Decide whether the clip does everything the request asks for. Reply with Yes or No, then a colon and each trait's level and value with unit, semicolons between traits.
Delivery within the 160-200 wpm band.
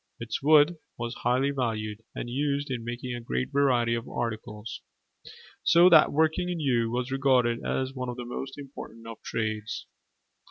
Yes: average, 165 wpm